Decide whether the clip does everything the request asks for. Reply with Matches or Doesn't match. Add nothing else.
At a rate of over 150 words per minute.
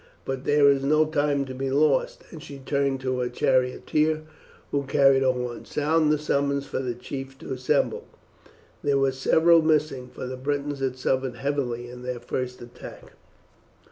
Matches